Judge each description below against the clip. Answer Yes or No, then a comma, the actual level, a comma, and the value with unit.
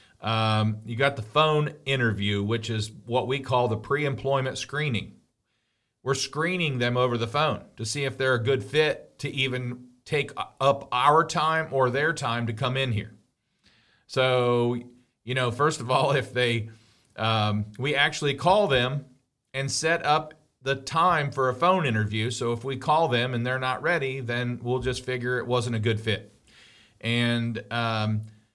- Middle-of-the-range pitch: No, low, 125 Hz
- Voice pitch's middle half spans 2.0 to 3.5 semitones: Yes, average, 2.9 semitones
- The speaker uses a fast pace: No, average, 175 wpm